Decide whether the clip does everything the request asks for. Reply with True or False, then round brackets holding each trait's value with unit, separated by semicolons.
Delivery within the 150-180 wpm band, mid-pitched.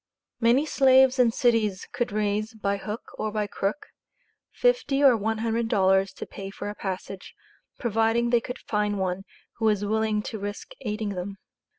False (170 wpm; 215 Hz)